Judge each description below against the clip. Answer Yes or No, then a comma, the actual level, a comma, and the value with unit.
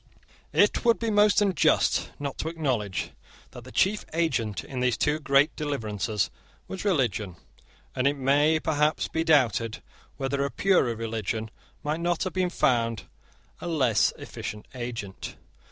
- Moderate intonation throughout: No, wide, 5.9 semitones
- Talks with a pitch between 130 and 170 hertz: Yes, medium, 140 Hz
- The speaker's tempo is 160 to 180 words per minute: No, average, 145 wpm